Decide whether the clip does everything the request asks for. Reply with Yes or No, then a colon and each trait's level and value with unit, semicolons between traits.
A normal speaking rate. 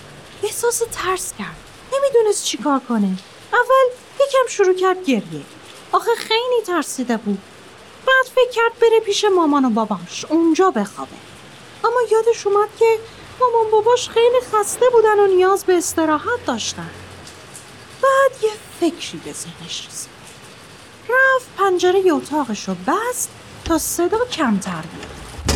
Yes: average, 130 wpm